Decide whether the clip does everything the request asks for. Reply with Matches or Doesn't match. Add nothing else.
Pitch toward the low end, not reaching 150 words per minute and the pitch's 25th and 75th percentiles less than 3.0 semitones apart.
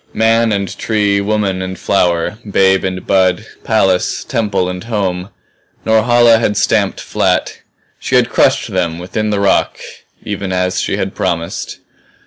Matches